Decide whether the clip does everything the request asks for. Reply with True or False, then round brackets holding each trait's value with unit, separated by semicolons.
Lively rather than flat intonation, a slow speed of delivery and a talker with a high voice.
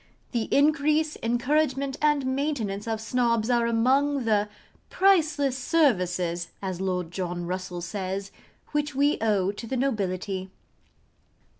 True (6.8 semitones; 120 wpm; 230 Hz)